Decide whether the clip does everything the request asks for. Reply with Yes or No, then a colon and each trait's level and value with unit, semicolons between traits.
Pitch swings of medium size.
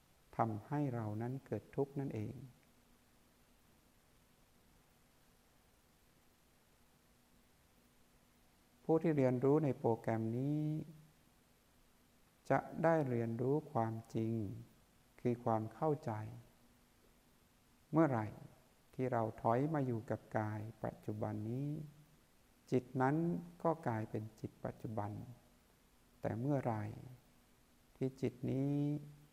Yes: average, 4.5 semitones